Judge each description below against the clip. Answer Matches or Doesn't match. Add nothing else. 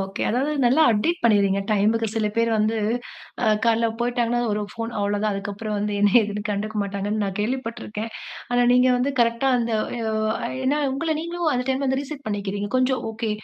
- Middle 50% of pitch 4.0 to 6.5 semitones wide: Doesn't match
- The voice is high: Matches